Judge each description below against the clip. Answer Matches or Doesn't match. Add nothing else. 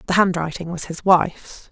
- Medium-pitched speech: Matches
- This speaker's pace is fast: Doesn't match